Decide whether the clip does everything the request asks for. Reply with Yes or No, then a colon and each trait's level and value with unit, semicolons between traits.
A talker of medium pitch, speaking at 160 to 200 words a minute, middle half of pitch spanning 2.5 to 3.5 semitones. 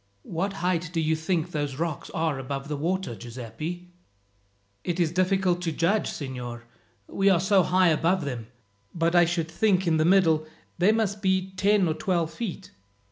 Yes: medium, 170 Hz; average, 175 wpm; average, 3.2 semitones